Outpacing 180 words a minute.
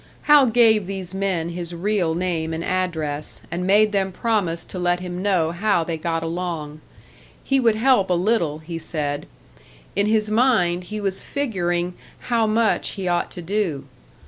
No: average, 170 wpm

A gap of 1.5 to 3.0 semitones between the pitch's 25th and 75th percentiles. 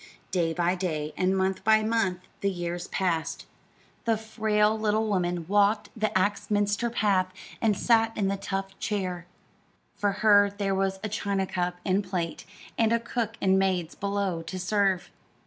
Yes: narrow, 2.4 semitones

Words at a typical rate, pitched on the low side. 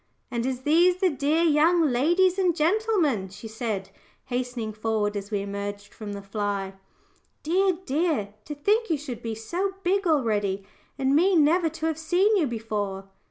No: average, 165 wpm; very high, 275 Hz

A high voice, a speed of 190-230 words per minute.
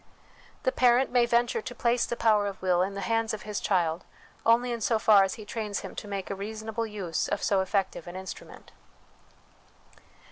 Yes: high, 210 Hz; average, 200 wpm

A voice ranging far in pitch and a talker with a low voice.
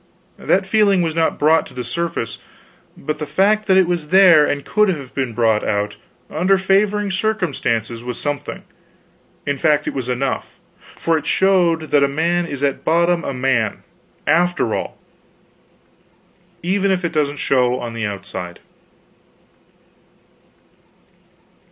No: wide, 6.2 semitones; medium, 155 Hz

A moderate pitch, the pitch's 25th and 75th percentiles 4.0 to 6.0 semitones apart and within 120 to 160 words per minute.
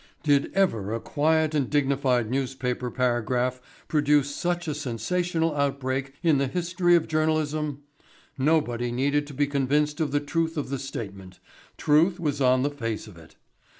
No: medium, 145 Hz; average, 3.4 semitones; average, 155 wpm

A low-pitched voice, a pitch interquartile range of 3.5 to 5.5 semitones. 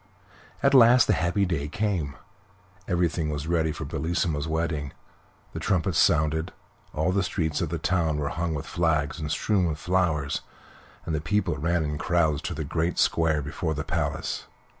No: very low, 80 Hz; narrow, 2.4 semitones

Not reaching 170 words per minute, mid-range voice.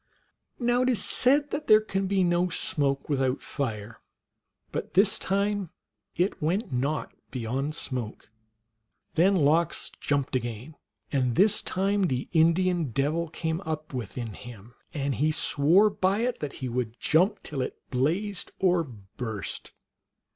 Yes: average, 140 wpm; medium, 155 Hz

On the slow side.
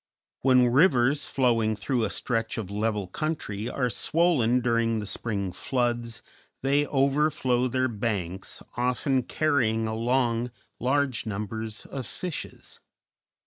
Yes: slow, 115 wpm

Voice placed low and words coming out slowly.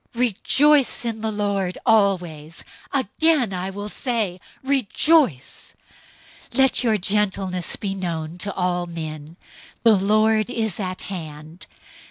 No: high, 200 Hz; slow, 125 wpm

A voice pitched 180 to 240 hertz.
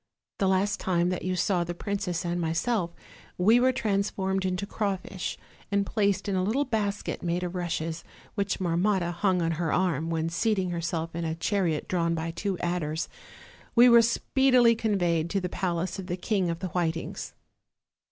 Yes: medium, 185 Hz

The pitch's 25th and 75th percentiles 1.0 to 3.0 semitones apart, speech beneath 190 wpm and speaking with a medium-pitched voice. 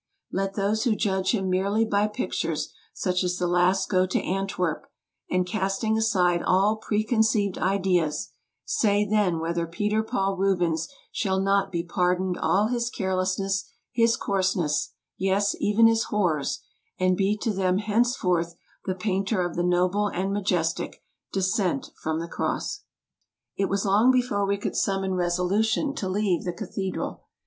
No: narrow, 2.5 semitones; average, 160 wpm; high, 195 Hz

